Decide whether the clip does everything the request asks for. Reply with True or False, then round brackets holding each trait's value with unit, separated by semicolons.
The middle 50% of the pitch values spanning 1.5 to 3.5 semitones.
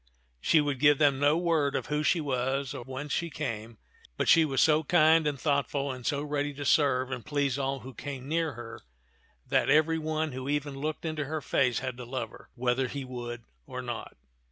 True (2.8 semitones)